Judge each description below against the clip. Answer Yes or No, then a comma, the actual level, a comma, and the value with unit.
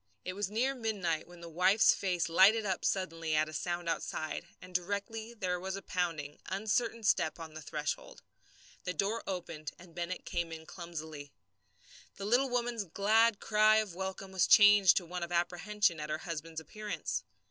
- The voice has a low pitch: No, medium, 180 Hz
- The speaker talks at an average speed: Yes, average, 175 wpm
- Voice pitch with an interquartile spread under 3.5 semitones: No, average, 3.9 semitones